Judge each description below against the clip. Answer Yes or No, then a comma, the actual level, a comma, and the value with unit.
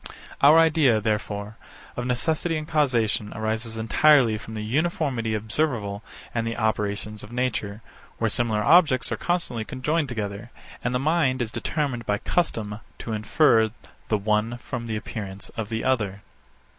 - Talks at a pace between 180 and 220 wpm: No, average, 150 wpm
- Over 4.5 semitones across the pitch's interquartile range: No, average, 4.2 semitones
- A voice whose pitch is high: No, low, 115 Hz